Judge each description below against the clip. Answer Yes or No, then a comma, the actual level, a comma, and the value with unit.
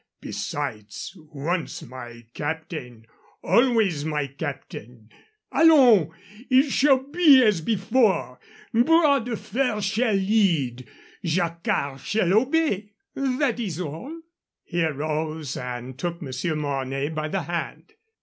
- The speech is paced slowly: Yes, slow, 110 wpm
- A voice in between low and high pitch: Yes, medium, 170 Hz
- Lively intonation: Yes, wide, 8.4 semitones